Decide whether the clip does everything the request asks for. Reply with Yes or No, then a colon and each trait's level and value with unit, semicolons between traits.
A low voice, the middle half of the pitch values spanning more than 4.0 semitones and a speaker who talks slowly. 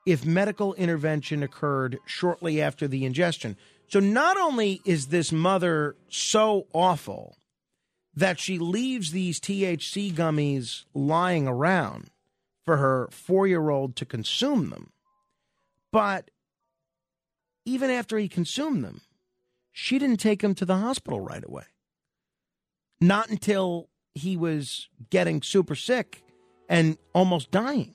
No: medium, 175 Hz; average, 5.2 semitones; slow, 120 wpm